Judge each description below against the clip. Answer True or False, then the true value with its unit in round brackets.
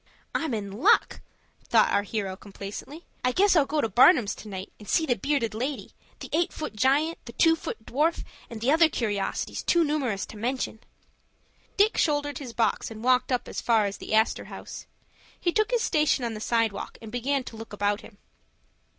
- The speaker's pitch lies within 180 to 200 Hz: False (245 Hz)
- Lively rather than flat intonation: True (5.8 semitones)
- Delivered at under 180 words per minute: False (195 wpm)